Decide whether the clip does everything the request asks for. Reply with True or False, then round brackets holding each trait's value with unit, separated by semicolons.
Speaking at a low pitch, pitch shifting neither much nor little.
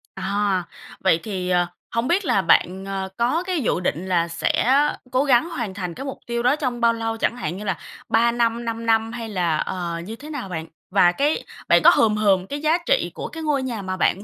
False (225 Hz; 5.0 semitones)